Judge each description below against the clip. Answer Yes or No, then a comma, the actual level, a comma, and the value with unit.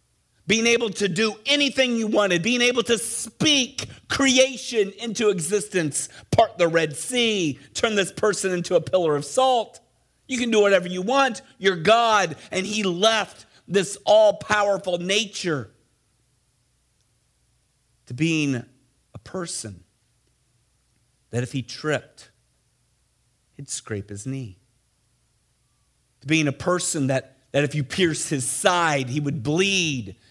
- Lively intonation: Yes, wide, 8.1 semitones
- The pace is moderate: No, slow, 130 wpm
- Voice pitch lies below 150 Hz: No, medium, 175 Hz